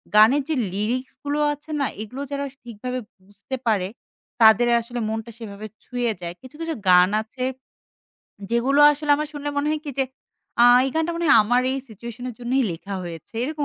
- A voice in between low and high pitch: No, high, 245 Hz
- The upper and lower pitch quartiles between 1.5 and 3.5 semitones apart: No, average, 4.7 semitones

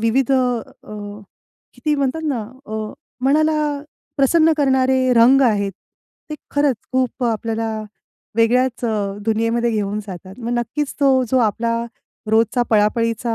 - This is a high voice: Yes, high, 235 Hz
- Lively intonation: No, average, 3.0 semitones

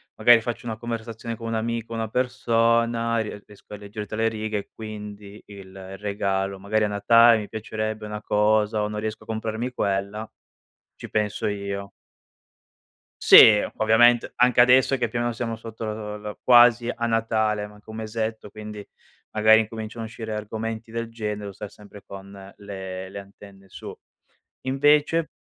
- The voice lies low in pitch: Yes, low, 110 Hz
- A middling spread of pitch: No, narrow, 1.8 semitones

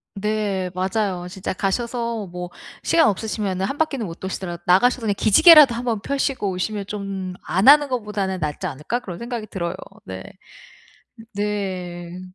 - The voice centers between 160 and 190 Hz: No, high, 200 Hz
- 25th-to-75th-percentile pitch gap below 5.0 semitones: Yes, average, 4.2 semitones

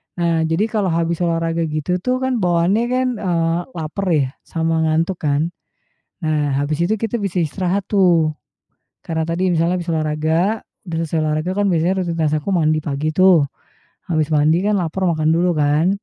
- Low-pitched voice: No, medium, 165 Hz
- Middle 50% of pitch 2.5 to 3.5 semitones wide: Yes, average, 2.9 semitones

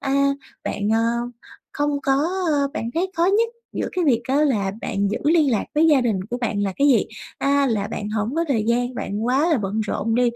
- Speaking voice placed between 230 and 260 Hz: Yes, very high, 250 Hz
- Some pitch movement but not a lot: Yes, average, 5.0 semitones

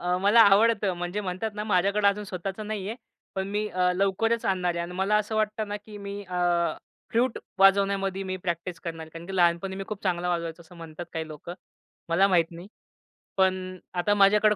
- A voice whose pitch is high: Yes, high, 195 Hz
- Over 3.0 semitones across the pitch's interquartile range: No, average, 2.7 semitones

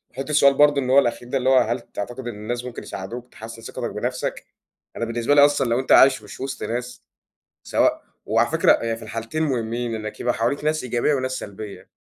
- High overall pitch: No, low, 120 Hz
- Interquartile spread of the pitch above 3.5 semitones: No, average, 2.9 semitones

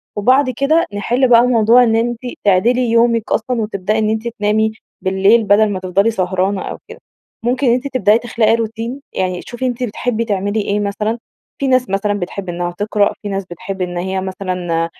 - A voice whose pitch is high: Yes, high, 215 Hz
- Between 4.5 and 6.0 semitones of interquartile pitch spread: No, average, 3.5 semitones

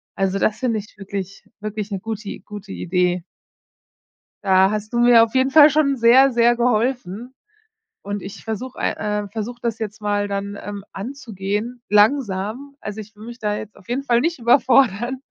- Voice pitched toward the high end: Yes, high, 215 Hz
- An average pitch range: Yes, average, 3.3 semitones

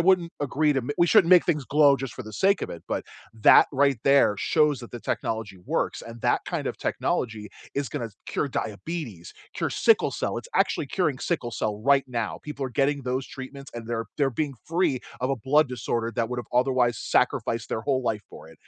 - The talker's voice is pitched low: Yes, low, 130 Hz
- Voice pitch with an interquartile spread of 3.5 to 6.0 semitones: Yes, average, 3.9 semitones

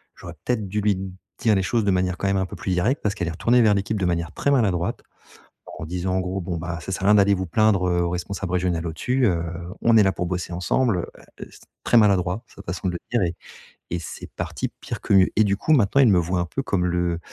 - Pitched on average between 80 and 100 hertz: Yes, very low, 95 Hz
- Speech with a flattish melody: No, average, 3.1 semitones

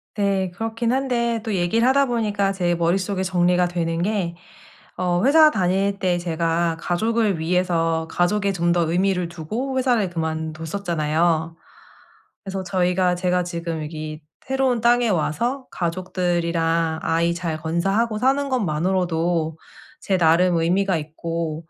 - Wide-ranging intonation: No, average, 3.4 semitones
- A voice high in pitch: No, medium, 180 Hz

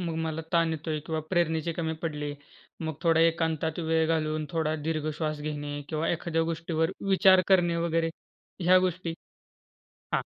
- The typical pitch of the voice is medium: Yes, medium, 160 Hz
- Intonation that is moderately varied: No, narrow, 1.2 semitones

